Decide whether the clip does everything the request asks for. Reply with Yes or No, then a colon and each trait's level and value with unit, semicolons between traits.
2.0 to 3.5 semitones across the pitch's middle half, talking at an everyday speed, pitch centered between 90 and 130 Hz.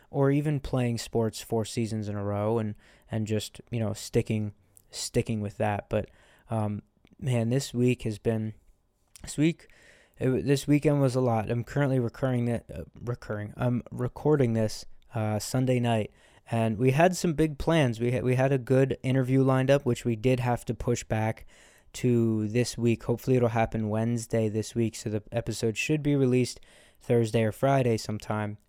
Yes: average, 2.9 semitones; average, 180 wpm; low, 120 Hz